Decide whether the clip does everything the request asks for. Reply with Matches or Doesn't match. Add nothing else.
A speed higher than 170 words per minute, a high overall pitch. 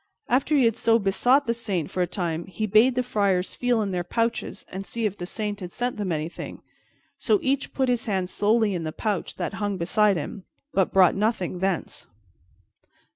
Matches